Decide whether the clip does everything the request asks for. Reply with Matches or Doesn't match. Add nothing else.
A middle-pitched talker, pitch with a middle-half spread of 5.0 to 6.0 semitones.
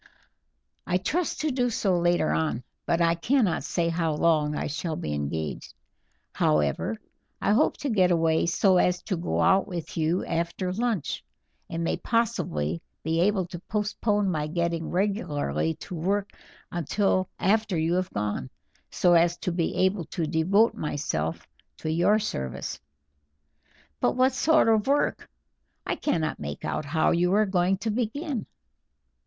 Doesn't match